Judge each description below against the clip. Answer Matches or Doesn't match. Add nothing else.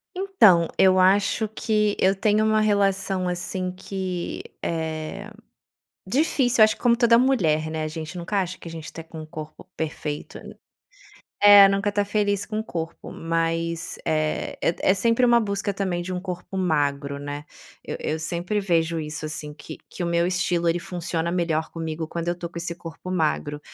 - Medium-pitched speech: Matches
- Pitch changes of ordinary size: Matches